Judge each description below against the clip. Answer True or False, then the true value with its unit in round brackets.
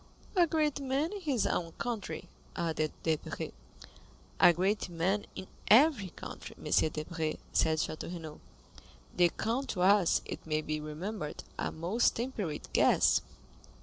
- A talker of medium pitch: True (180 Hz)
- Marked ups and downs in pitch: True (7.1 semitones)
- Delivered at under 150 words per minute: True (135 wpm)